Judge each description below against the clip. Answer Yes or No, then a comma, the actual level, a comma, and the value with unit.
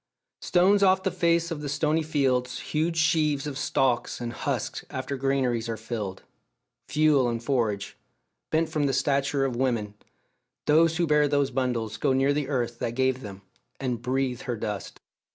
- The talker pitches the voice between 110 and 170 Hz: Yes, low, 135 Hz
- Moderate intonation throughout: Yes, average, 4.0 semitones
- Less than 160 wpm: No, average, 170 wpm